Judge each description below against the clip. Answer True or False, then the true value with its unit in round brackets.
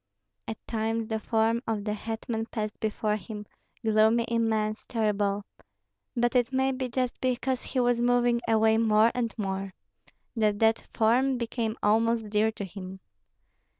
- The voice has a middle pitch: False (225 Hz)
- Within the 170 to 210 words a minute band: False (150 wpm)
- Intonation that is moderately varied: False (1.8 semitones)